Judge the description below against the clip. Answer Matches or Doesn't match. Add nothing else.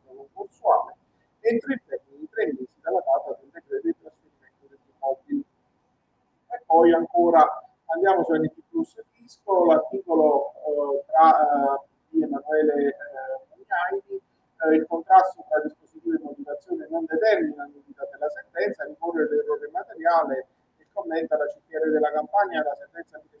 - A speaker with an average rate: Matches